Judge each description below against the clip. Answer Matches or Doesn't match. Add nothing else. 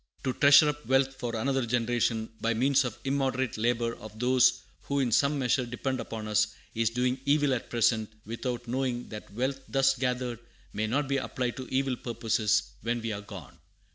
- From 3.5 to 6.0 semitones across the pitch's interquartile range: Doesn't match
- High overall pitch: Doesn't match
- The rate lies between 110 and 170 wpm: Doesn't match